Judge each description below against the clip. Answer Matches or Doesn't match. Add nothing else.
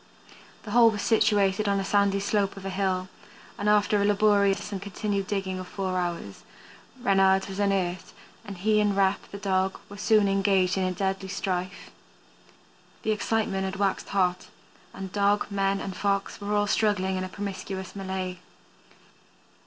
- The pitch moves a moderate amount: Doesn't match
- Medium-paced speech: Matches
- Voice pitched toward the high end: Matches